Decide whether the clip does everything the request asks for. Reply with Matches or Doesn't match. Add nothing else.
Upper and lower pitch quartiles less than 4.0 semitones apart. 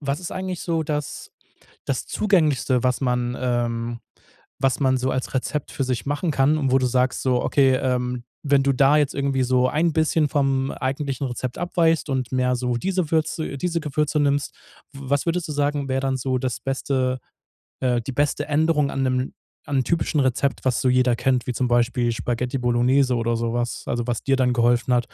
Matches